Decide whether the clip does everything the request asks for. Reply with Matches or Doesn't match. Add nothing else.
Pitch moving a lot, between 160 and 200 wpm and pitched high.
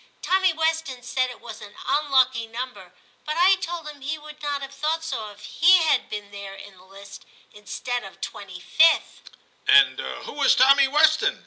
Matches